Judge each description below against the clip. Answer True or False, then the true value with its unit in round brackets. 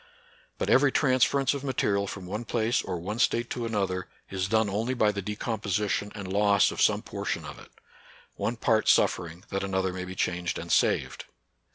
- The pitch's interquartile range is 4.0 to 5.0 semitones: False (3.4 semitones)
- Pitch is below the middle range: True (105 Hz)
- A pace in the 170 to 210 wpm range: True (190 wpm)